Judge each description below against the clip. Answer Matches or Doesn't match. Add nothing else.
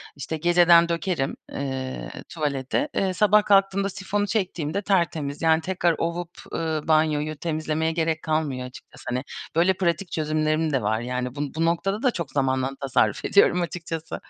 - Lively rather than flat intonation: Doesn't match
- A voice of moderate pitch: Matches